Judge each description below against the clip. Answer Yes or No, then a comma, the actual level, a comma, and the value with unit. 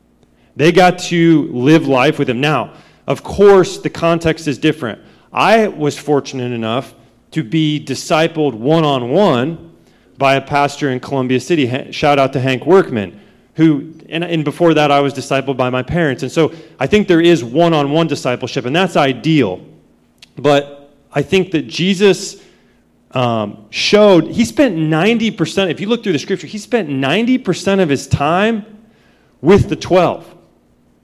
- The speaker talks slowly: No, average, 160 wpm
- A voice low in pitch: No, medium, 150 Hz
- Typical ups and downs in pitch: Yes, average, 4.7 semitones